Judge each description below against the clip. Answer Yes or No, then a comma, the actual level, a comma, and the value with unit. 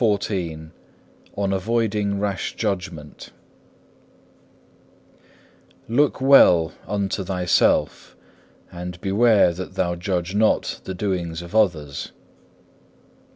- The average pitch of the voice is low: Yes, very low, 95 Hz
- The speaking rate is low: Yes, slow, 90 wpm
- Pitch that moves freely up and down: No, average, 3.0 semitones